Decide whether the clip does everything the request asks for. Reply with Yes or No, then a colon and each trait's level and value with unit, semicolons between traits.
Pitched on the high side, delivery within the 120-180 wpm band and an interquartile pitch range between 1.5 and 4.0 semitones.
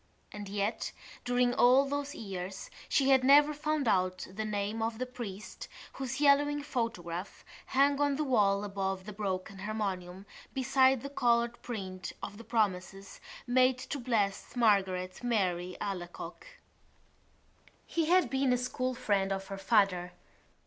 No: high, 220 Hz; average, 140 wpm; average, 5.1 semitones